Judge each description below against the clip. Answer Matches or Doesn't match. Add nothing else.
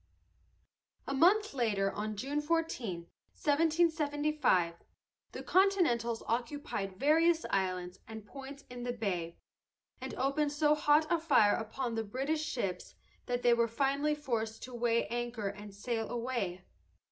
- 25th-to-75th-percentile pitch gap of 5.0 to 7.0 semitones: Matches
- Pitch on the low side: Doesn't match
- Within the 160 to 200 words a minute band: Doesn't match